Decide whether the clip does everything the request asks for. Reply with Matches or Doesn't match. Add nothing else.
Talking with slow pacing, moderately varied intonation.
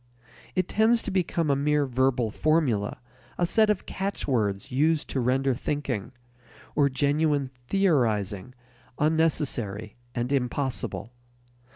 Matches